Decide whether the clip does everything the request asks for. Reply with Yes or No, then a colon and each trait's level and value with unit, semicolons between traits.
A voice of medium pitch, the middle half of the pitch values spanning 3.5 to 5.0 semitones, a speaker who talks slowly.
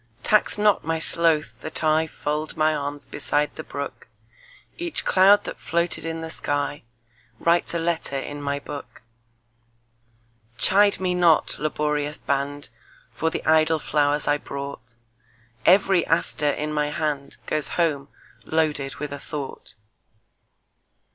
No: medium, 150 Hz; average, 2.8 semitones; slow, 115 wpm